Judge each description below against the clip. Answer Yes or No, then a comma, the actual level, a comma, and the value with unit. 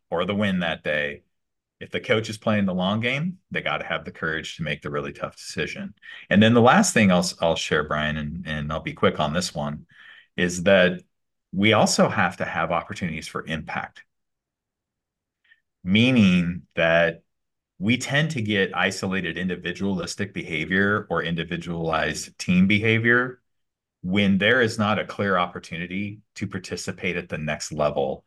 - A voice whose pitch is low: Yes, very low, 95 Hz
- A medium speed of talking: Yes, average, 165 wpm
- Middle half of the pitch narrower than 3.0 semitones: No, average, 4.2 semitones